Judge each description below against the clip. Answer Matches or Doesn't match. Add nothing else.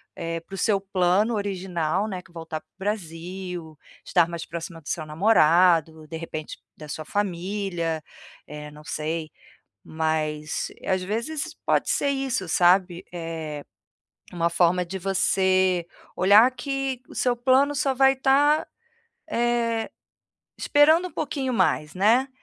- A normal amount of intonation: Doesn't match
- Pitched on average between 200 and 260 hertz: Doesn't match